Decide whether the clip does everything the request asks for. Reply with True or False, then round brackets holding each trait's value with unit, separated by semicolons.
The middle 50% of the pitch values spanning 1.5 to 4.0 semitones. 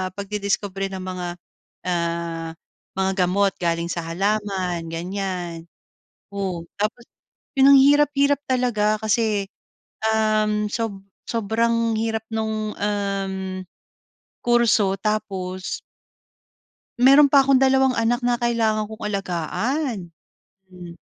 True (3.6 semitones)